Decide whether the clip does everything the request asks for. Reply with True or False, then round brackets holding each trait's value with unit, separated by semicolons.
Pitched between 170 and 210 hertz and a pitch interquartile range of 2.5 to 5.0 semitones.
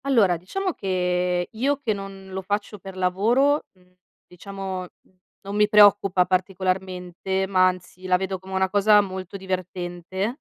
False (190 Hz; 1.9 semitones)